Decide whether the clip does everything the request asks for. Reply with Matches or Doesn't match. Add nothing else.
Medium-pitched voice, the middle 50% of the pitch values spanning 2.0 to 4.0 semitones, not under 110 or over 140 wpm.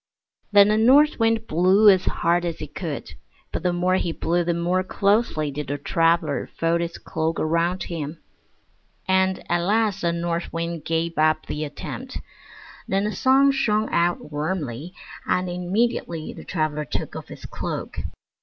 Doesn't match